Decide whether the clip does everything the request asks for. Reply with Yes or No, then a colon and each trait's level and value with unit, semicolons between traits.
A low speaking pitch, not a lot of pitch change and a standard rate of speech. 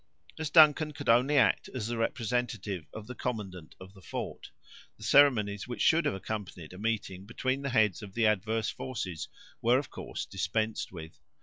No: low, 110 Hz; average, 4.5 semitones; average, 180 wpm